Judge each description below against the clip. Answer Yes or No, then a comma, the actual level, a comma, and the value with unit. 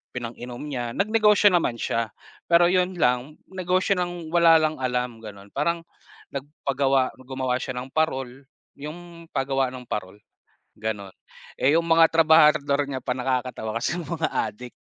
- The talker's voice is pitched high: No, medium, 140 Hz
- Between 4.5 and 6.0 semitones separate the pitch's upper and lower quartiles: Yes, average, 4.9 semitones